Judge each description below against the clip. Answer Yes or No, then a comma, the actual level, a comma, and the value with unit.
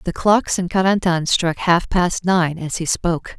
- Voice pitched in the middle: Yes, medium, 175 Hz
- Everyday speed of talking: Yes, average, 195 wpm